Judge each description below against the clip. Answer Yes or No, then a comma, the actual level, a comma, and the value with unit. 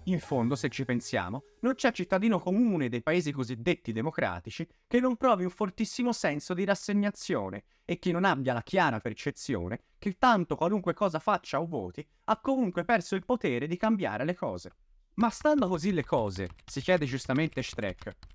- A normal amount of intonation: No, wide, 7.9 semitones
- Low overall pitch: No, medium, 175 Hz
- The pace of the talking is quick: Yes, fast, 175 wpm